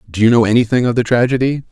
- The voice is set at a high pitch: No, low, 120 Hz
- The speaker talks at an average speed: No, fast, 245 wpm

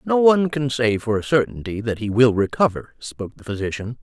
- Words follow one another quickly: Yes, fast, 210 wpm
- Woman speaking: No, male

